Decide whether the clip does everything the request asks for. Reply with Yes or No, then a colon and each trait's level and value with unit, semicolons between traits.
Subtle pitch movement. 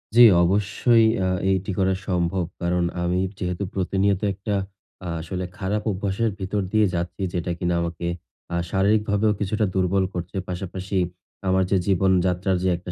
Yes: narrow, 2.0 semitones